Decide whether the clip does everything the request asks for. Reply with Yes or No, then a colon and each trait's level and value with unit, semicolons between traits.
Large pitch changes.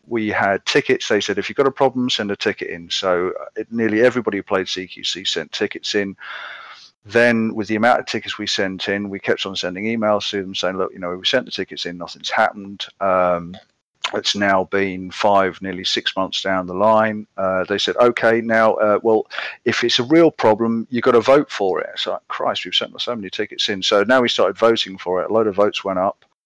No: average, 3.1 semitones